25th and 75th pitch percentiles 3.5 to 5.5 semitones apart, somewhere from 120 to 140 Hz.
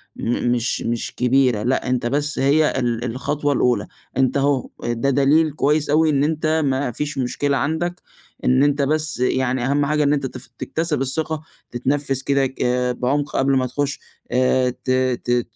No: narrow, 2.6 semitones; low, 135 Hz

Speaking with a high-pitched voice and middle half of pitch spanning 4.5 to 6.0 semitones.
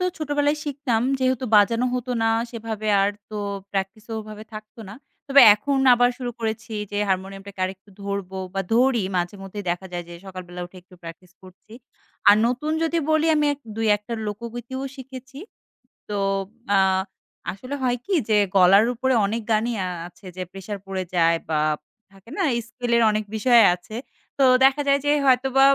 Yes: high, 220 Hz; average, 4.8 semitones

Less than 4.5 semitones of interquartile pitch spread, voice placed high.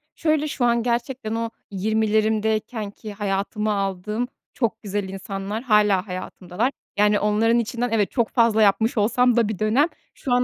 Yes: narrow, 2.4 semitones; high, 220 Hz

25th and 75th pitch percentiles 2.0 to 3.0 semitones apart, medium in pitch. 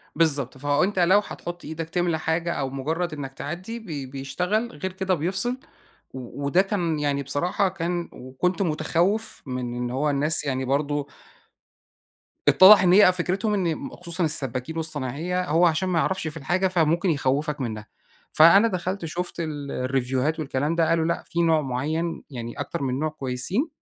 No: average, 4.4 semitones; medium, 160 Hz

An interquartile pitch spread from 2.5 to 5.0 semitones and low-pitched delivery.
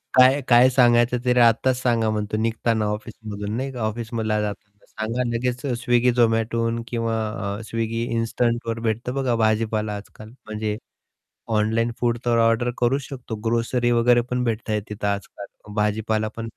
No: narrow, 1.9 semitones; low, 115 Hz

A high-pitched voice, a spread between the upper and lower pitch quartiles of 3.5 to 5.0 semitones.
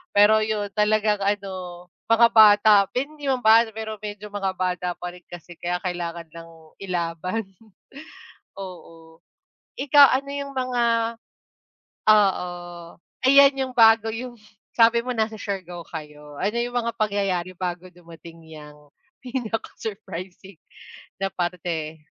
Yes: high, 200 Hz; average, 4.4 semitones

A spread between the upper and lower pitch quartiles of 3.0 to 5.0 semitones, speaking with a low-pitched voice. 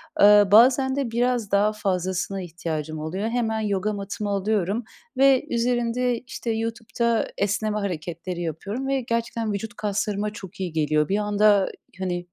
No: average, 3.6 semitones; high, 210 Hz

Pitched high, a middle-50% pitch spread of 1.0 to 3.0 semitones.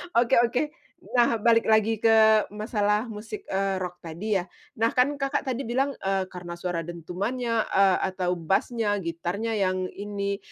No: high, 210 Hz; average, 3.7 semitones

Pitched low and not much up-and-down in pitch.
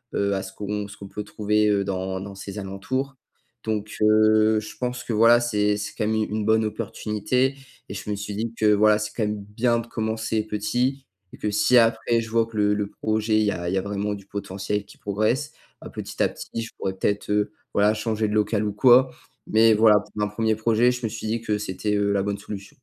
Yes: low, 105 Hz; narrow, 1.5 semitones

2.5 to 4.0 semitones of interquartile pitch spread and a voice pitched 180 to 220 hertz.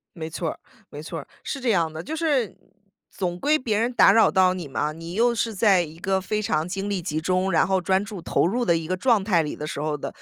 No: average, 4.9 semitones; medium, 185 Hz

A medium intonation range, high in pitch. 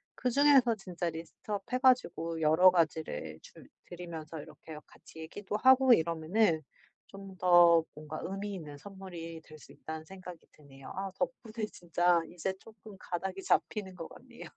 No: average, 4.0 semitones; medium, 180 Hz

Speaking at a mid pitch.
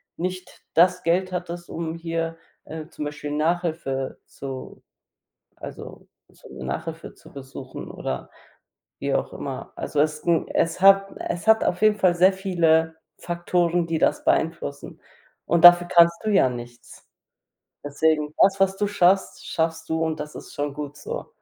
Yes: medium, 165 Hz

